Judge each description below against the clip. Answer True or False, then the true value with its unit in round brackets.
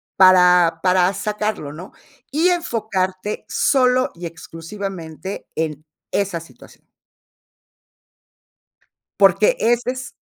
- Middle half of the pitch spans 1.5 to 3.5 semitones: False (4.1 semitones)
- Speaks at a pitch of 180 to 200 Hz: True (190 Hz)